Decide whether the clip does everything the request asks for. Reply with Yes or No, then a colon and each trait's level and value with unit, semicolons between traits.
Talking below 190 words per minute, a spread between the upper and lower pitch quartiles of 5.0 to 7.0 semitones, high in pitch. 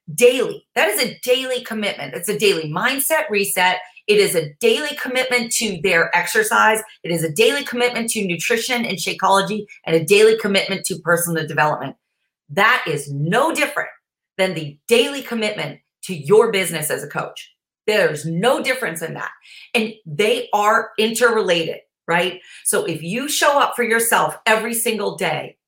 Yes: average, 160 wpm; wide, 5.5 semitones; high, 215 Hz